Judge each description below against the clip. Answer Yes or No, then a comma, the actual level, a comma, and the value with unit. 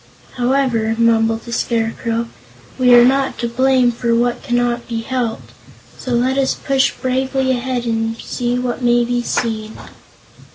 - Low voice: No, high, 240 Hz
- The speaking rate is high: No, average, 150 wpm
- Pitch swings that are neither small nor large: No, narrow, 1.8 semitones